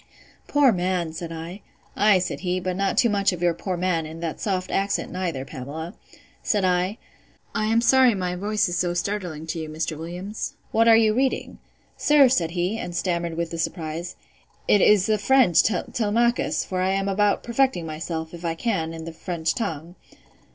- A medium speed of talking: Yes, average, 185 wpm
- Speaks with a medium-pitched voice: Yes, medium, 180 Hz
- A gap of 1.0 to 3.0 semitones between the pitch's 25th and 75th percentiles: No, average, 4.0 semitones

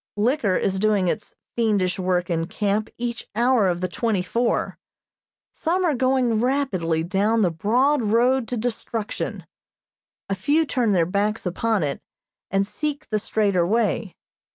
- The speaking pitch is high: Yes, high, 215 Hz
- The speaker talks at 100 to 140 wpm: No, average, 150 wpm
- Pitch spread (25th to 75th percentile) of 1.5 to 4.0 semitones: No, average, 4.5 semitones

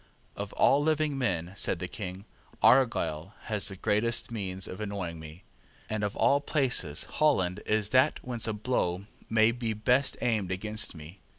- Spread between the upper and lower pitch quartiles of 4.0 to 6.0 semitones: Yes, average, 4.9 semitones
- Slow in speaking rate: No, average, 165 wpm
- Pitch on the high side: No, low, 105 Hz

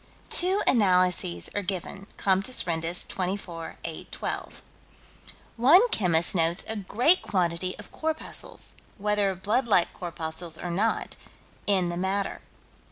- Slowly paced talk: Yes, slow, 115 wpm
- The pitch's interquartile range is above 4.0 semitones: No, average, 3.3 semitones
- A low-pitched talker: No, high, 190 Hz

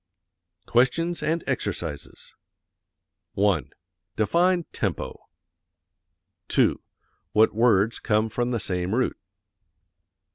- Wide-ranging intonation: Yes, wide, 6.9 semitones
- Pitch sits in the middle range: No, low, 115 Hz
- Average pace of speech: No, slow, 80 wpm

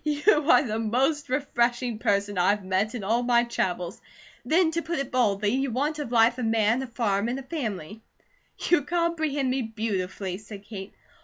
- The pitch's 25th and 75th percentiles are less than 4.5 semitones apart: No, average, 5.0 semitones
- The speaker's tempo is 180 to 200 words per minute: Yes, average, 185 wpm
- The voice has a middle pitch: No, high, 235 Hz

